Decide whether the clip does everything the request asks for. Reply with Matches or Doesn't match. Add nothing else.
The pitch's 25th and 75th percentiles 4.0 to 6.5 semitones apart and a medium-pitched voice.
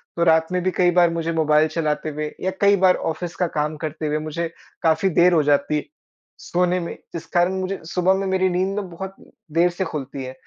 Doesn't match